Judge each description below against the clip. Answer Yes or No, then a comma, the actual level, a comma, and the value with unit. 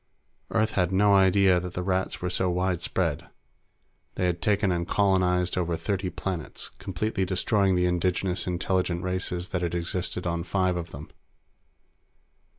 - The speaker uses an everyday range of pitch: No, narrow, 1.4 semitones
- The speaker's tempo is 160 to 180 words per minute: No, average, 150 wpm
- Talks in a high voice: No, very low, 90 Hz